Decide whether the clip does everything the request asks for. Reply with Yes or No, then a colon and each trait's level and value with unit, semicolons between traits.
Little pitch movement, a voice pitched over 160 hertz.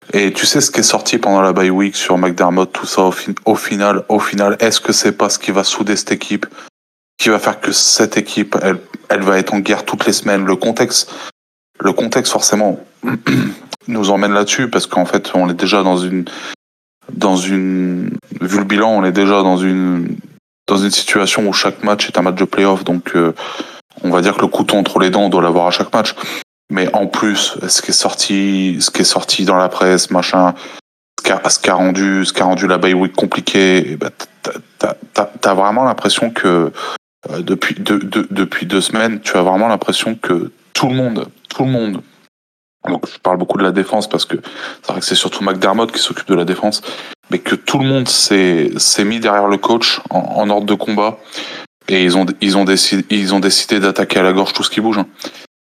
No: narrow, 1.9 semitones; very low, 95 Hz